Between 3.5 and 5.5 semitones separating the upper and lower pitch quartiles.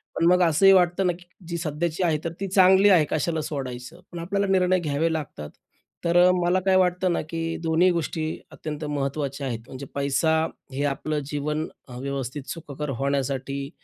Yes: average, 4.0 semitones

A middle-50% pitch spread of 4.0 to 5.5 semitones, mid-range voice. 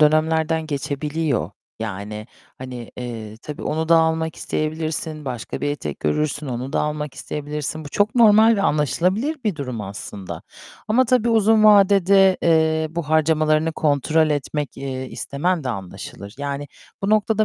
No: average, 3.6 semitones; medium, 155 Hz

